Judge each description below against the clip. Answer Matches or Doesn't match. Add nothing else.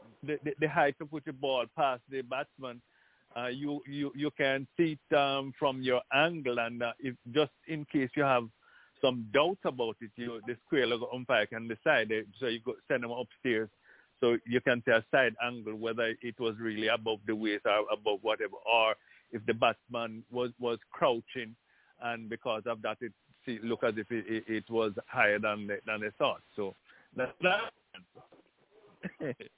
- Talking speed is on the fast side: Doesn't match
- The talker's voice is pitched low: Matches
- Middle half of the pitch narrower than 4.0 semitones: Matches